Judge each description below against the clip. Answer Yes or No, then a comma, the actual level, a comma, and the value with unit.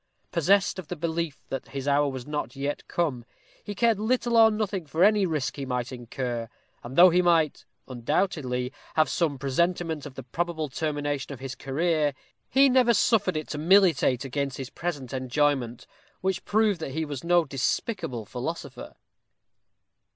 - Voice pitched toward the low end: No, medium, 150 Hz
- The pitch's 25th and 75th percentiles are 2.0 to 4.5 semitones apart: No, average, 5.1 semitones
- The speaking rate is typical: Yes, average, 165 wpm